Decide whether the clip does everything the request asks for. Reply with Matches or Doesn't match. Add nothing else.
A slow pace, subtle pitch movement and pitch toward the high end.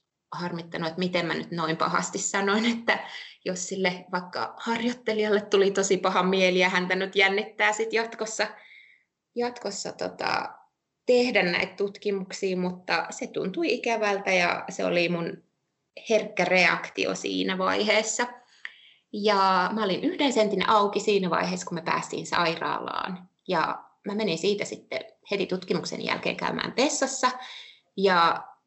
Doesn't match